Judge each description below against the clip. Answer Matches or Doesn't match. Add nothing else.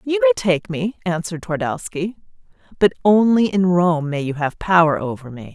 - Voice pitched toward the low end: Doesn't match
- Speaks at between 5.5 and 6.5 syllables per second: Doesn't match